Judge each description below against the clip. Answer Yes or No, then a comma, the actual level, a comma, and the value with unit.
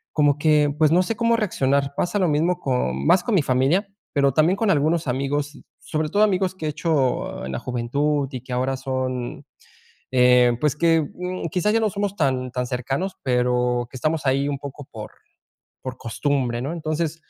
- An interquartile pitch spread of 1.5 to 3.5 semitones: No, average, 4.7 semitones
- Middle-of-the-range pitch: Yes, medium, 145 Hz